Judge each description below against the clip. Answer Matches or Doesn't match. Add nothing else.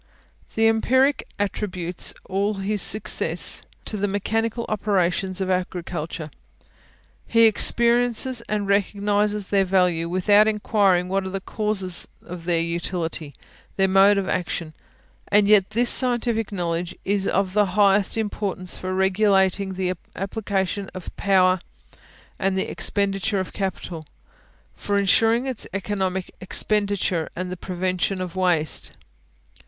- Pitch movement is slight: Matches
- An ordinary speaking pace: Doesn't match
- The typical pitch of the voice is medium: Doesn't match